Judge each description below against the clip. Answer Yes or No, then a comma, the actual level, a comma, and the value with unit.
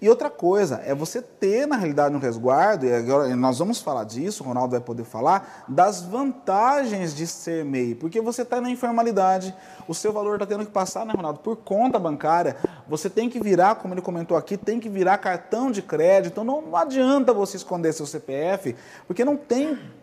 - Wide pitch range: Yes, wide, 6.4 semitones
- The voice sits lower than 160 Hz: No, high, 190 Hz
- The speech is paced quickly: Yes, fast, 200 wpm